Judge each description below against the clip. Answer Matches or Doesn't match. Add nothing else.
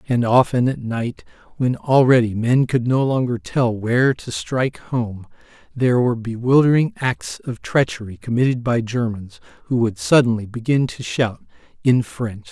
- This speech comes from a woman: Doesn't match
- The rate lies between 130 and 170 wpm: Matches